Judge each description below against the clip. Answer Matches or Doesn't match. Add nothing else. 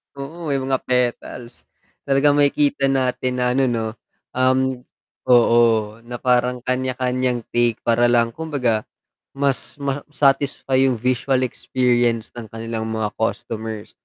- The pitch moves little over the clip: Matches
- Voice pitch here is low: Matches